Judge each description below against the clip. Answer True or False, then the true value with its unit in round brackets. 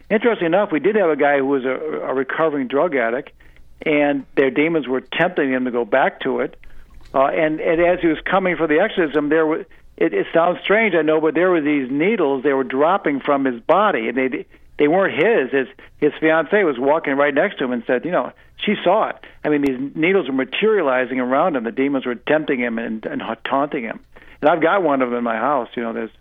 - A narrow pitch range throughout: False (3.8 semitones)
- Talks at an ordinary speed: False (230 wpm)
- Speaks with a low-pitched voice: False (145 Hz)